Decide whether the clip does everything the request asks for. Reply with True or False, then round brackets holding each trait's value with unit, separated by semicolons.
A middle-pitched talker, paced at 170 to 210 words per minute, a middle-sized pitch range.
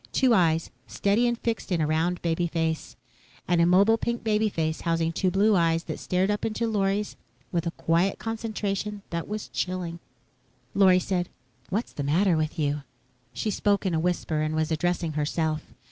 True (180 Hz; 175 wpm; 4.0 semitones)